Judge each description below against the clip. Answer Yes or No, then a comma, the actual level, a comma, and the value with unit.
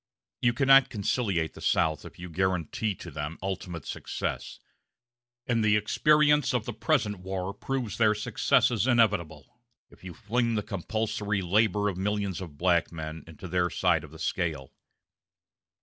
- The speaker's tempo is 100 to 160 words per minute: Yes, average, 150 wpm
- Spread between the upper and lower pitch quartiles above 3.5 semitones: Yes, average, 4.5 semitones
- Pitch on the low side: Yes, very low, 95 Hz